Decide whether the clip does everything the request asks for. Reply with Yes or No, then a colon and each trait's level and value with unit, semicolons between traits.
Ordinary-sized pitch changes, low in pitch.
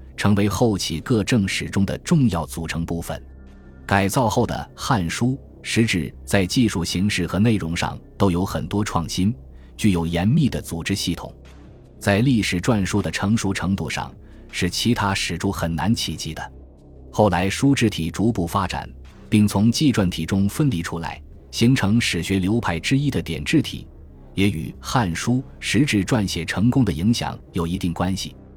Yes: average, 4.8 semitones; very low, 95 Hz